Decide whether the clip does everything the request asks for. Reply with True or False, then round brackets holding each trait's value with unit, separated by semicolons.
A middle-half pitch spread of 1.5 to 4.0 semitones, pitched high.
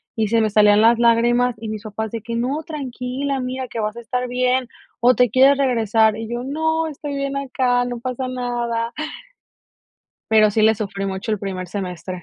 True (2.7 semitones; 235 Hz)